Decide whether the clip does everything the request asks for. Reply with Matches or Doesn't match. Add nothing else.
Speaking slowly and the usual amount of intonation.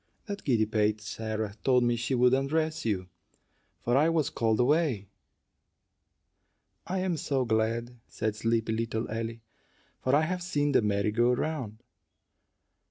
Doesn't match